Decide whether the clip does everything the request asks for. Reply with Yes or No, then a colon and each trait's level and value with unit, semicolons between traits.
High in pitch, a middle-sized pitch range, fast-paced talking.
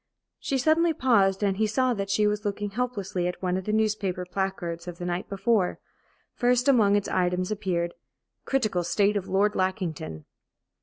No: high, 200 Hz; average, 3.1 semitones; average, 170 wpm